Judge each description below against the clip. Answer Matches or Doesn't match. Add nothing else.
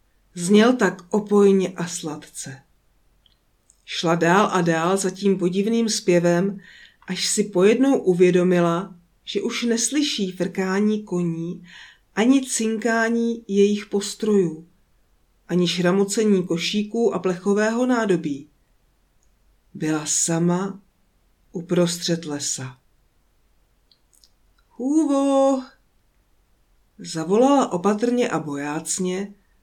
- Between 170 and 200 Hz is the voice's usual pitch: Matches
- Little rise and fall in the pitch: Doesn't match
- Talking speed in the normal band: Doesn't match